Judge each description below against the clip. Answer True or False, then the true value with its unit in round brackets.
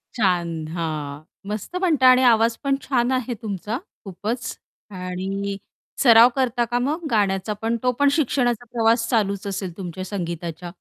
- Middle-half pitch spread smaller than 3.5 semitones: False (4.7 semitones)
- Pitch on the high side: True (220 Hz)